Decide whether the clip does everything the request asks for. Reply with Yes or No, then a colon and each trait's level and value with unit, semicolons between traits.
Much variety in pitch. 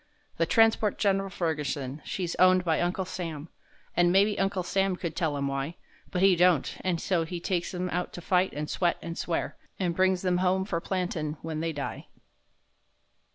No: narrow, 2.4 semitones